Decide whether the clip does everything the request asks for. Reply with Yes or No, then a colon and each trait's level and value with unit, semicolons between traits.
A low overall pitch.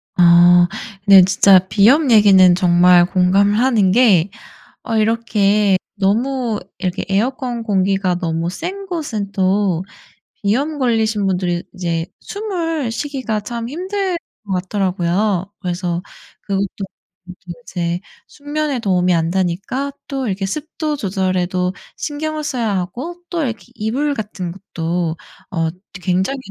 No: high, 200 Hz